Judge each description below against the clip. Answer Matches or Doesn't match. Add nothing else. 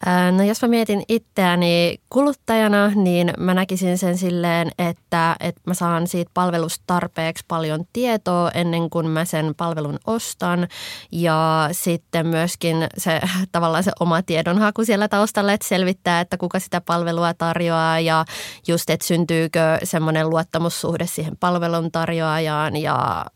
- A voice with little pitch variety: Matches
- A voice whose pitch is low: Doesn't match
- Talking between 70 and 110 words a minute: Doesn't match